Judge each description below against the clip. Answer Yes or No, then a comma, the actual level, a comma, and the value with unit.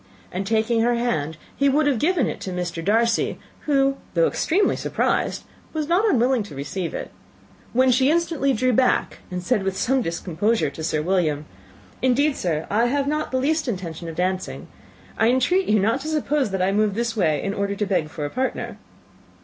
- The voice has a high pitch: Yes, high, 225 Hz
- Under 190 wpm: No, average, 195 wpm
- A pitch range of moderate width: No, wide, 6.8 semitones